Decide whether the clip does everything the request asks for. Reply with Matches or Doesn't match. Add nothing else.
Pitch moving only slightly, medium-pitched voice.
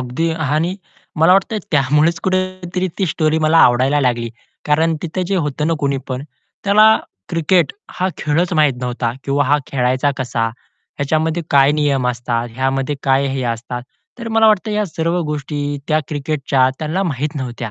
Doesn't match